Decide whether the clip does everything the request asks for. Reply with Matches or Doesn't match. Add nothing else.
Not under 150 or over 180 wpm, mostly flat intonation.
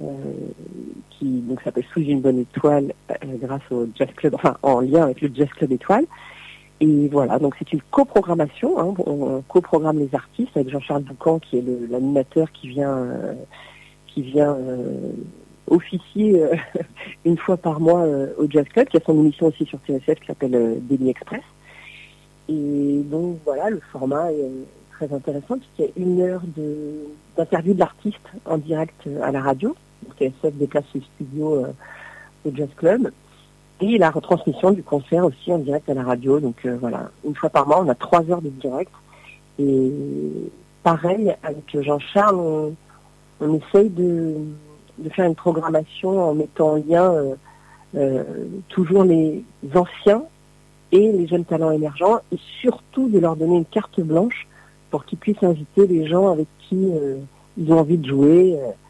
Doesn't match